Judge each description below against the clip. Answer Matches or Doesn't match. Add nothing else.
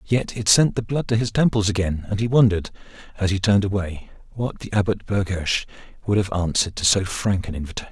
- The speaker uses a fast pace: Matches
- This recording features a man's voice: Matches